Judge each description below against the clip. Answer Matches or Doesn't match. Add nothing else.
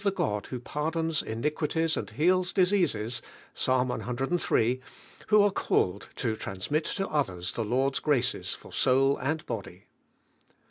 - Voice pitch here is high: Doesn't match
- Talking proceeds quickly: Doesn't match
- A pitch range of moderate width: Doesn't match